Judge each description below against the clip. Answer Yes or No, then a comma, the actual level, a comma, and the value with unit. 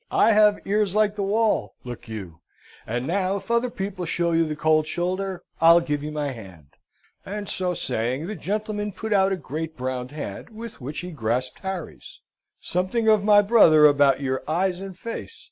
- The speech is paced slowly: No, average, 185 wpm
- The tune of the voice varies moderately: No, wide, 6.2 semitones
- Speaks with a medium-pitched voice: Yes, medium, 175 Hz